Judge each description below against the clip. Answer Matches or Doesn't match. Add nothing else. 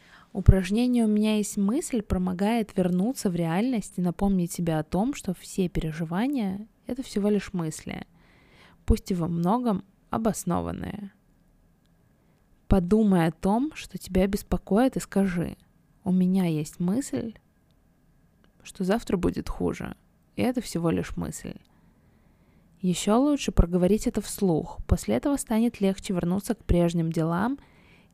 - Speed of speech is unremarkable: Matches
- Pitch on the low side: Doesn't match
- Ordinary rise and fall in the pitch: Matches